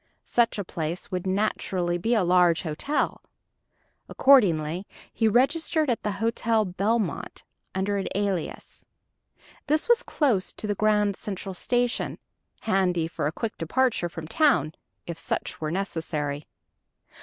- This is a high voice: Yes, high, 195 Hz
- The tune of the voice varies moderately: Yes, average, 4.8 semitones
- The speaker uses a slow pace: Yes, slow, 130 wpm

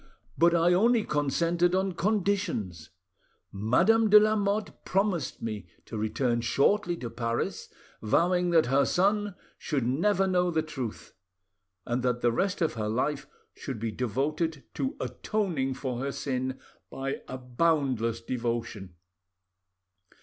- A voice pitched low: No, medium, 145 Hz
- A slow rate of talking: Yes, slow, 130 wpm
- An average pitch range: No, wide, 7.3 semitones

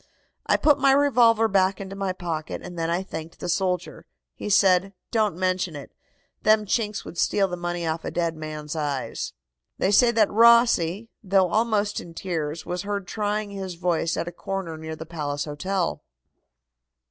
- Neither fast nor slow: Yes, average, 175 wpm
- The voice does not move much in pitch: No, average, 3.8 semitones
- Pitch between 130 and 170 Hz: No, medium, 185 Hz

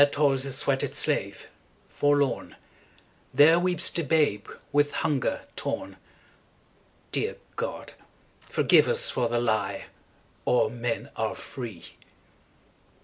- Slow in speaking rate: Yes, slow, 95 wpm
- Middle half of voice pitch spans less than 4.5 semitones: Yes, average, 3.6 semitones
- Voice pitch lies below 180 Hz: Yes, medium, 140 Hz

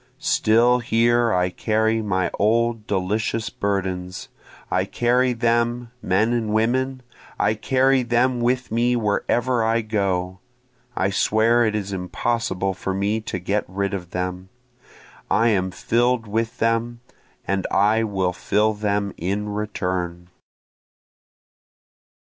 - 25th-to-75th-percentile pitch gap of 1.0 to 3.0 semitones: No, average, 3.4 semitones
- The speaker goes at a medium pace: No, slow, 125 wpm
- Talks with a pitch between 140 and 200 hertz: No, low, 110 Hz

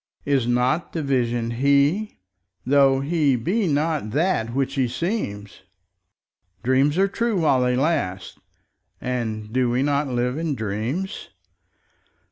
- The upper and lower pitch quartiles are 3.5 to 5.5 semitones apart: Yes, average, 4.6 semitones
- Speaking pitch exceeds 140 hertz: No, low, 130 Hz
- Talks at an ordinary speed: No, slow, 120 wpm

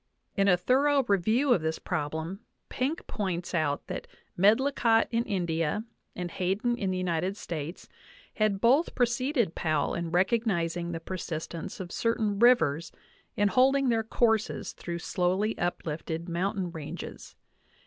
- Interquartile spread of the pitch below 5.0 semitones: No, average, 5.3 semitones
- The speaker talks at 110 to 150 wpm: Yes, average, 140 wpm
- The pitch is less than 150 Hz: No, high, 190 Hz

